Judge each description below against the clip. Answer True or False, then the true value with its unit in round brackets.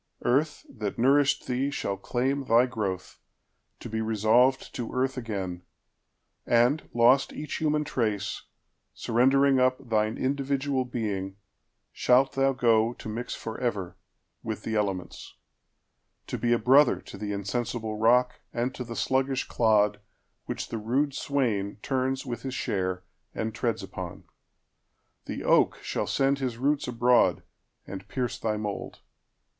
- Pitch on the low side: True (120 Hz)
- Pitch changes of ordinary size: True (3.6 semitones)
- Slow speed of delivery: True (120 wpm)